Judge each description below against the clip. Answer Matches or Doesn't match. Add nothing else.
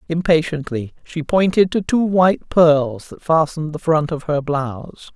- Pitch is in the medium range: Matches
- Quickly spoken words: Doesn't match